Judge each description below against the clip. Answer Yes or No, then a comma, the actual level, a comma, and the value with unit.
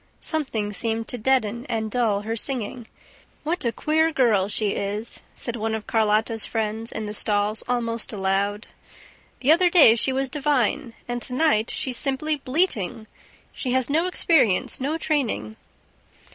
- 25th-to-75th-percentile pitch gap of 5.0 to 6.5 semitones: No, average, 4.2 semitones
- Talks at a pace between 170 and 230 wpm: No, average, 155 wpm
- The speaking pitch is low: No, high, 235 Hz